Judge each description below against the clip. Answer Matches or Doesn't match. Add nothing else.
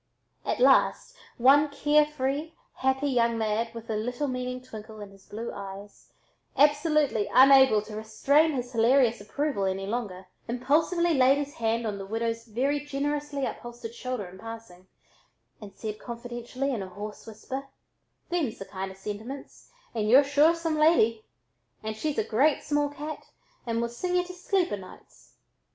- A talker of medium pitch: Doesn't match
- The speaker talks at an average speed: Matches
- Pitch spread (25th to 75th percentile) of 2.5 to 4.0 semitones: Doesn't match